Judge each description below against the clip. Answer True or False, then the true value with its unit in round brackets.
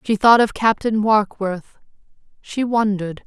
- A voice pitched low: False (210 Hz)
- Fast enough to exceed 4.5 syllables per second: False (4.3 syllables/s)